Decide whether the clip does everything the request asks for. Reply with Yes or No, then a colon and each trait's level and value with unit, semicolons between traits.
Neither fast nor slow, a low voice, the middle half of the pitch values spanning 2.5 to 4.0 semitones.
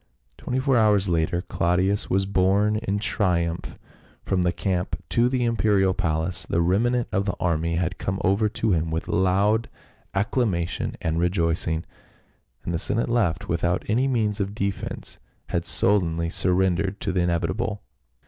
Yes: average, 150 wpm; very low, 95 Hz; average, 3.6 semitones